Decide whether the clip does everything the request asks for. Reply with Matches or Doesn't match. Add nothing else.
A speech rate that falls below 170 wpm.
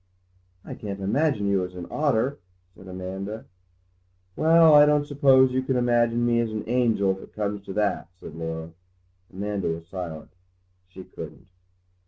Matches